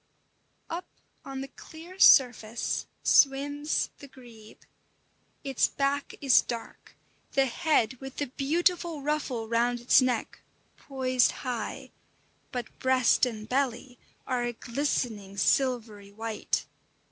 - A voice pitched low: No, very high, 255 Hz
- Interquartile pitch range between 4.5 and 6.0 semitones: No, average, 3.1 semitones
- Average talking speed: No, slow, 110 wpm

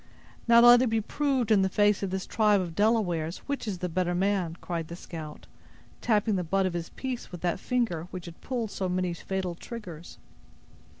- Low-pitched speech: No, high, 190 Hz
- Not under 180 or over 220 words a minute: Yes, average, 200 wpm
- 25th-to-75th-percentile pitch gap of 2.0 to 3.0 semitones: No, average, 4.3 semitones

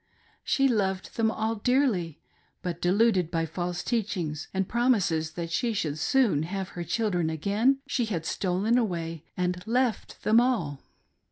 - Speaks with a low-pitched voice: No, high, 190 Hz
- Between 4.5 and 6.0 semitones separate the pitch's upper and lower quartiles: Yes, average, 5.3 semitones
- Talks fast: No, average, 155 wpm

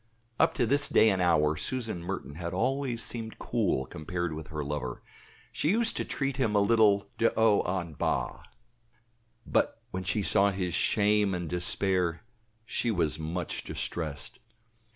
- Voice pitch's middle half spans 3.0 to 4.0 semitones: No, average, 5.0 semitones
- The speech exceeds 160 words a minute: No, average, 155 wpm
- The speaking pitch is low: Yes, very low, 95 Hz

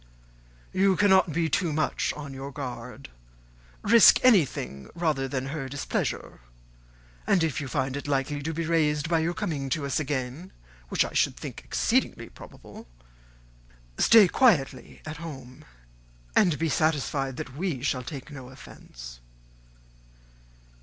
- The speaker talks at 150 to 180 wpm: No, average, 140 wpm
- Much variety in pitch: No, average, 3.7 semitones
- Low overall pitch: No, medium, 145 Hz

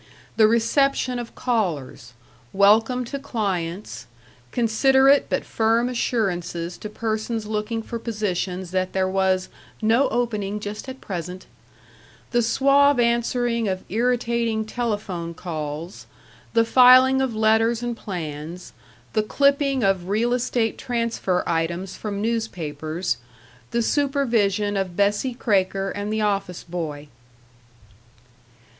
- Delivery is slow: Yes, slow, 115 wpm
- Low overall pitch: No, high, 215 Hz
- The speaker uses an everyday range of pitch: Yes, average, 4.2 semitones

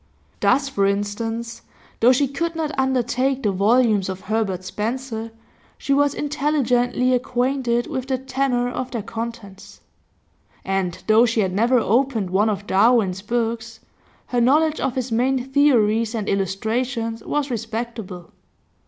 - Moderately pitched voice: No, high, 235 Hz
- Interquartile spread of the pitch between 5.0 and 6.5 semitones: No, average, 3.5 semitones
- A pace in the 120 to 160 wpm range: Yes, slow, 135 wpm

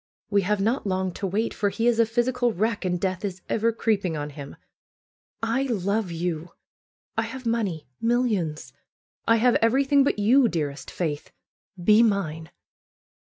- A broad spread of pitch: No, average, 4.7 semitones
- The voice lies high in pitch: Yes, high, 205 Hz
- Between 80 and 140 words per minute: No, average, 165 wpm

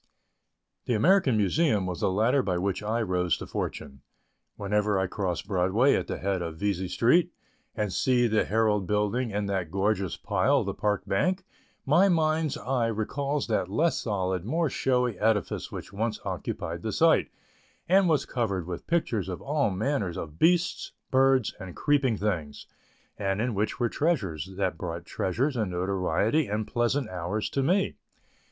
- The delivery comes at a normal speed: Yes, average, 165 wpm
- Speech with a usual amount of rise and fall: No, wide, 5.9 semitones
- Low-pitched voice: Yes, low, 105 Hz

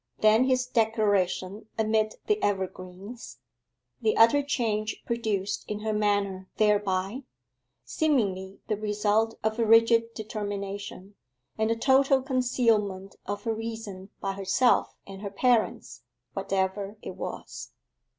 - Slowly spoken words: Yes, slow, 120 wpm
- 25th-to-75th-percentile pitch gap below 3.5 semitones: Yes, narrow, 2.5 semitones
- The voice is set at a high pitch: Yes, high, 215 Hz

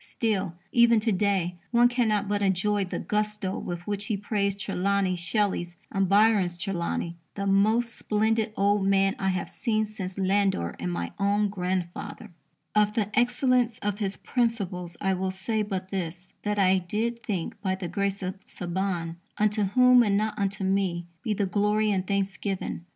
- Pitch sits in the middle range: No, high, 200 Hz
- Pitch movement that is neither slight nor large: No, narrow, 2.2 semitones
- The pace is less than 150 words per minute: No, average, 165 wpm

